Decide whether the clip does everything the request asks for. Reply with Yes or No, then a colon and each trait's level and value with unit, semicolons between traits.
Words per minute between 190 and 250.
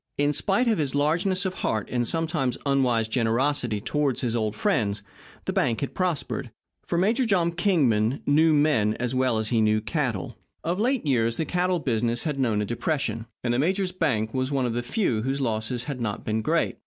Yes: average, 200 wpm